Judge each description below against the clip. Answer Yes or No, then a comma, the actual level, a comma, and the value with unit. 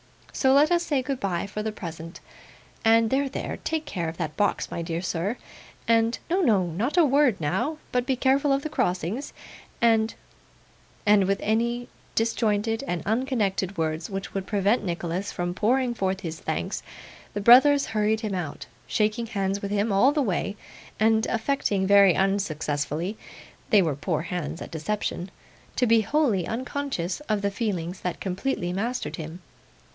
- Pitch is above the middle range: Yes, high, 205 Hz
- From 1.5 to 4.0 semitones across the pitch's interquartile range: No, average, 5.2 semitones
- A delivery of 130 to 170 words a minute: Yes, average, 165 wpm